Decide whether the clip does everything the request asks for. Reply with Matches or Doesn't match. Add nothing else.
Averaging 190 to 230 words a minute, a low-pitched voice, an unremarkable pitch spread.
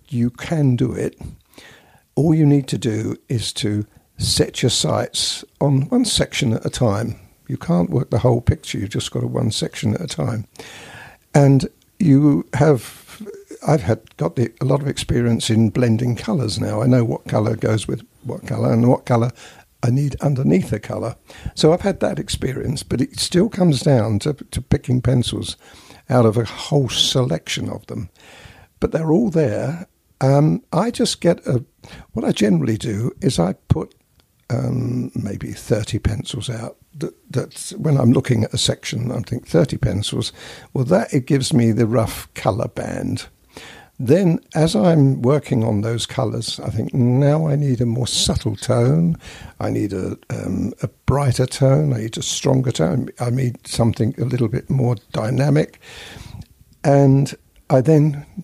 Doesn't match